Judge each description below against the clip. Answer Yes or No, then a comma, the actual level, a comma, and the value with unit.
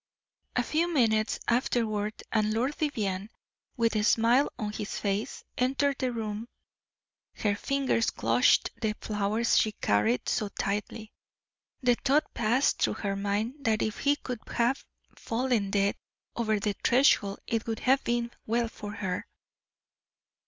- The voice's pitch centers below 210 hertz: No, high, 225 Hz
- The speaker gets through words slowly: No, average, 145 wpm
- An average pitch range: Yes, average, 3.0 semitones